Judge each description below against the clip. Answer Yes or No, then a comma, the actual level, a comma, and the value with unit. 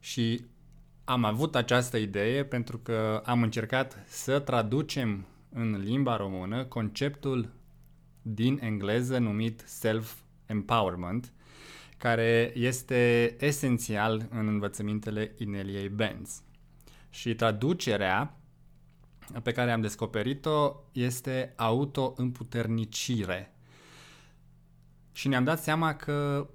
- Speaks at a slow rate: Yes, slow, 90 wpm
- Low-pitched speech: Yes, low, 115 Hz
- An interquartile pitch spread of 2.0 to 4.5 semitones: Yes, average, 3.3 semitones